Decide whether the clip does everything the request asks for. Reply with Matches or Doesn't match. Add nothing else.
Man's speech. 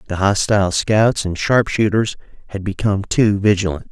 Matches